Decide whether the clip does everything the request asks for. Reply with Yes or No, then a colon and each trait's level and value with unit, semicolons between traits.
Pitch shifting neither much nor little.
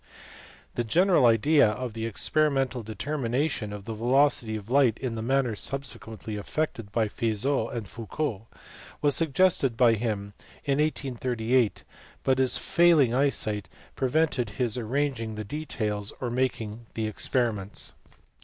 Yes: average, 4.0 semitones